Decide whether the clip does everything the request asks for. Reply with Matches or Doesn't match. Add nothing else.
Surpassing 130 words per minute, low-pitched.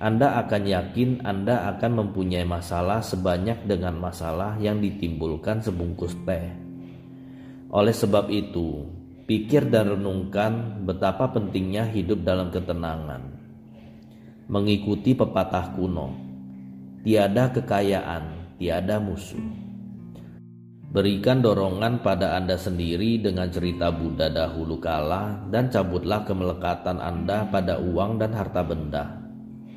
Doesn't match